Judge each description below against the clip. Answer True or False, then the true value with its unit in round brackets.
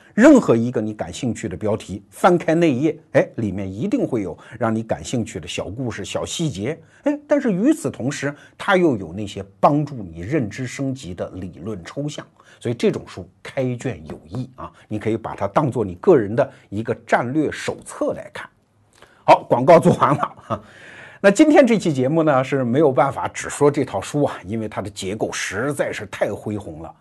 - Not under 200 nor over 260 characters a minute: False (280 characters per minute)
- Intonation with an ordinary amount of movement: False (6.9 semitones)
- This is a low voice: True (130 Hz)